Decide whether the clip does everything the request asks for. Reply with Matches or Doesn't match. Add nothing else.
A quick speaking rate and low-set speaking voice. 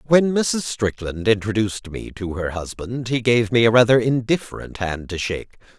Doesn't match